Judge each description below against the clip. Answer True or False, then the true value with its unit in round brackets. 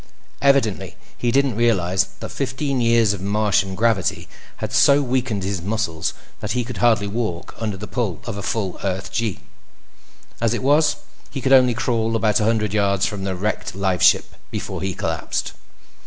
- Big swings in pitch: False (3.7 semitones)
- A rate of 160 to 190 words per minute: True (170 wpm)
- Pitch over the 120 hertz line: False (110 Hz)